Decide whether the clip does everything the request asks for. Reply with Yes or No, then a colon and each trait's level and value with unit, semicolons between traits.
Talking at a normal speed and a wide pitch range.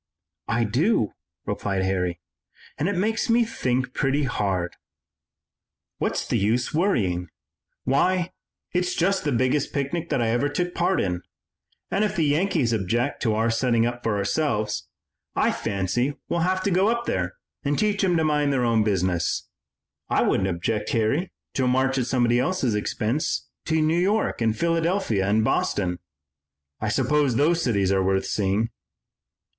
Yes: average, 160 wpm; wide, 8.0 semitones